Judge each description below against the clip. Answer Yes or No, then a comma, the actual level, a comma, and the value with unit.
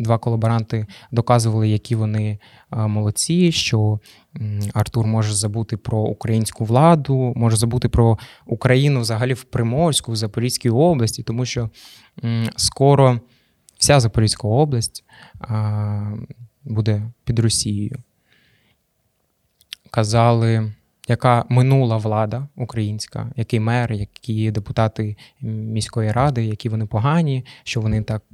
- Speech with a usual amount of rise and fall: No, narrow, 2.2 semitones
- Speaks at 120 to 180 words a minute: No, slow, 105 wpm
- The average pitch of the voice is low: Yes, low, 115 Hz